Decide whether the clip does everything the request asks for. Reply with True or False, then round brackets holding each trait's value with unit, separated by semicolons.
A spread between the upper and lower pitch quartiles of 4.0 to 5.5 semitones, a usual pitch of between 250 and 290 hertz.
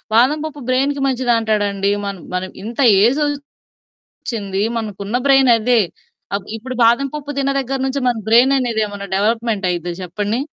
False (4.4 semitones; 230 Hz)